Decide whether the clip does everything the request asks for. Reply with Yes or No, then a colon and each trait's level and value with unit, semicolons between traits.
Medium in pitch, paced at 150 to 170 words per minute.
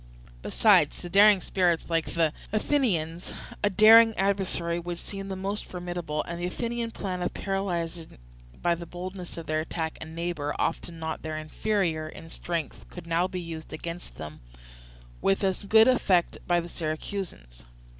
Yes: medium, 175 Hz; average, 160 wpm